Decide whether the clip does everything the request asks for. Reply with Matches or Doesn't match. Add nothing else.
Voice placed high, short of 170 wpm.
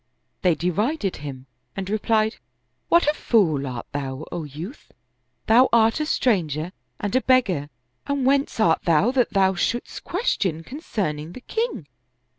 Matches